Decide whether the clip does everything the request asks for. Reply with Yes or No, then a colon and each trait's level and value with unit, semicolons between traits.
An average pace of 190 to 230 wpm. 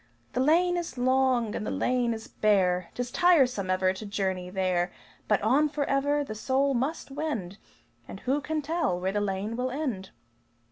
No: average, 175 wpm